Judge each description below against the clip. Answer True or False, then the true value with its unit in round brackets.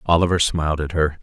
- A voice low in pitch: True (80 Hz)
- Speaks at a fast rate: False (195 wpm)